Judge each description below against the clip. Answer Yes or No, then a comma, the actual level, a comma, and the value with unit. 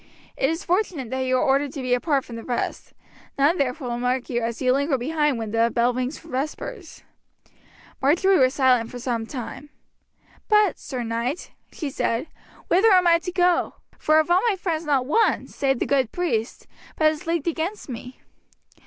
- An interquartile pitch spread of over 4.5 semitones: Yes, average, 5.1 semitones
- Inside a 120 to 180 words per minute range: No, average, 190 wpm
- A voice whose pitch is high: Yes, very high, 275 Hz